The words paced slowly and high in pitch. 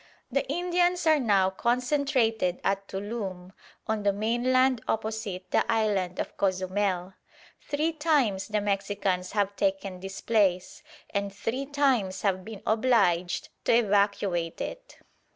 Yes: slow, 125 wpm; high, 205 Hz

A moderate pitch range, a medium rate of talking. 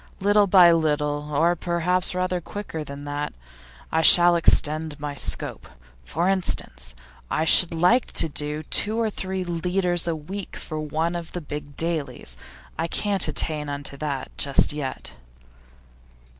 Yes: average, 3.4 semitones; average, 145 wpm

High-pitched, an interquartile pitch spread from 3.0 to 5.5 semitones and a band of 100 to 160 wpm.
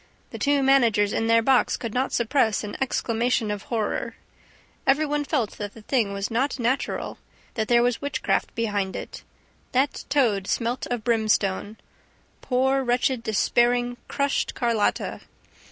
Yes: high, 240 Hz; average, 3.4 semitones; average, 145 wpm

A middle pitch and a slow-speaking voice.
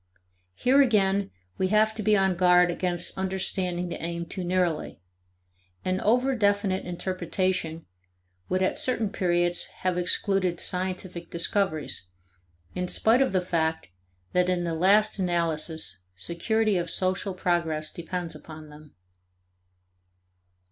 Yes: medium, 180 Hz; slow, 125 wpm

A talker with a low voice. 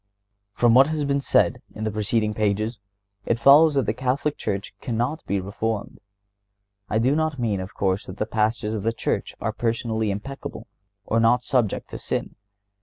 Yes: low, 115 Hz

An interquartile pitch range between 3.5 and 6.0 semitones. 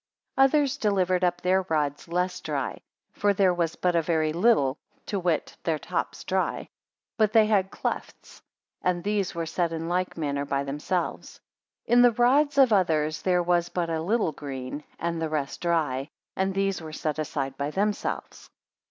Yes: average, 4.0 semitones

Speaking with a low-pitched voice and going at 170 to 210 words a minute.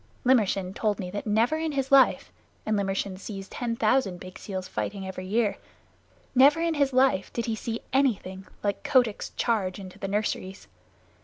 No: high, 210 Hz; average, 180 wpm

